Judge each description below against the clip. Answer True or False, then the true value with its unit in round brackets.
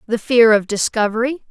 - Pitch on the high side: True (230 Hz)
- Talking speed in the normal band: True (160 wpm)